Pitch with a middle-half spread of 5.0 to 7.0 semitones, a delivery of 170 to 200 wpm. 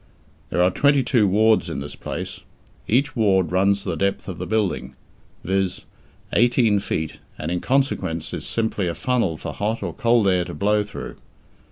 No: average, 4.1 semitones; average, 175 wpm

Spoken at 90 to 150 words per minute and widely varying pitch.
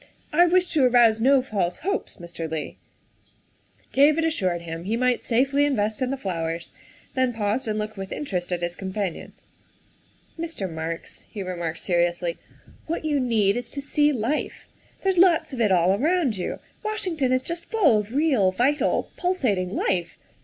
No: average, 170 wpm; wide, 8.0 semitones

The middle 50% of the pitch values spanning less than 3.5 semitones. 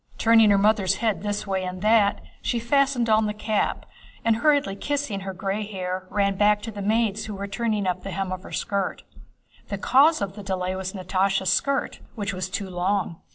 Yes: narrow, 2.5 semitones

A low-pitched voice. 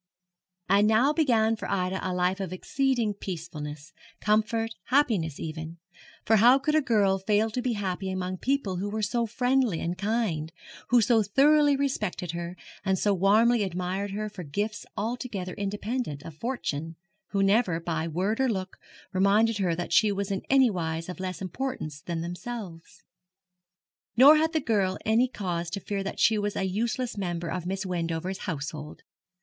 No: high, 200 Hz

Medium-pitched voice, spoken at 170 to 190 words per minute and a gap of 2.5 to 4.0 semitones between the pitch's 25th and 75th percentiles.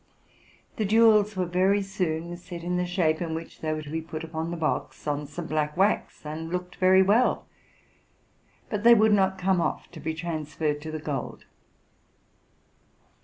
Yes: medium, 175 Hz; average, 175 wpm; average, 3.3 semitones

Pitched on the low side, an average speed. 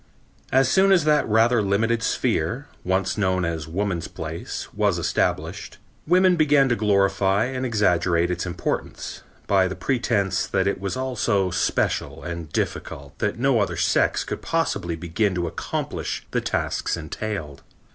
Yes: low, 100 Hz; average, 150 wpm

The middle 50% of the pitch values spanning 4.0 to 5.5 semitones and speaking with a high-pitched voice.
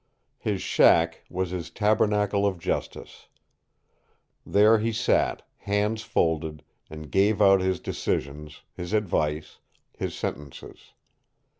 No: average, 4.7 semitones; very low, 95 Hz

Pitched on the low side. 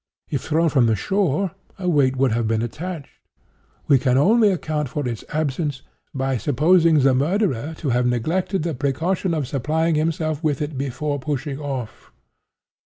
No: medium, 145 Hz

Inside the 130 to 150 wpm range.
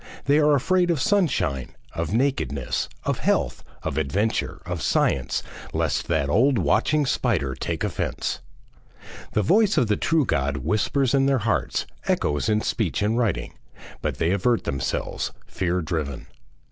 Yes: average, 145 wpm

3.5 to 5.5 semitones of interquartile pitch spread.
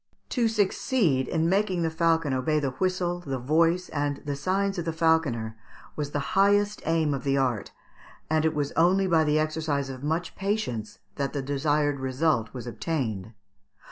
Yes: average, 4.2 semitones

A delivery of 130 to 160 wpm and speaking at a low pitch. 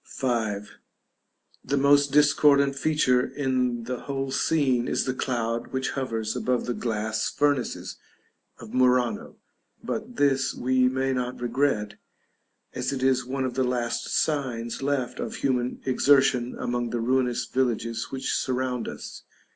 Yes: average, 140 wpm; low, 130 Hz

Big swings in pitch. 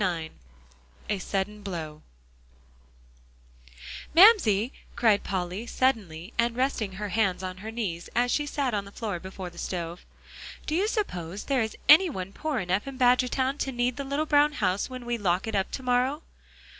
Yes: wide, 5.8 semitones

